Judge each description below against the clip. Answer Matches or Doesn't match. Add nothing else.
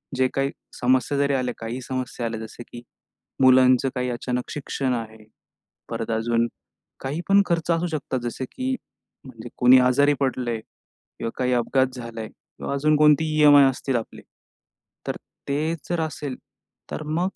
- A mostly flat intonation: Doesn't match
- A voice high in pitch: Doesn't match